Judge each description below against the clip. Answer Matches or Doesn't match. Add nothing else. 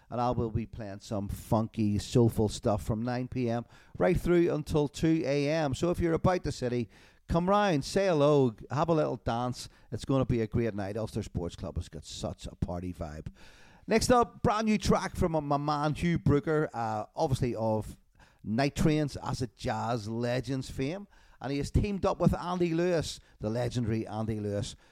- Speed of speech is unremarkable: Matches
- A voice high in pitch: Doesn't match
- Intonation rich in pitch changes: Matches